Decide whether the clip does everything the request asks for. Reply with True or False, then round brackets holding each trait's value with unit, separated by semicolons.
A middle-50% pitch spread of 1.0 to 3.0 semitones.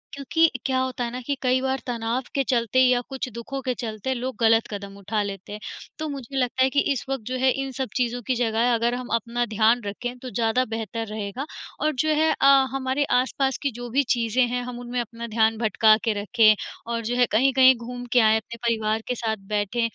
True (2.5 semitones)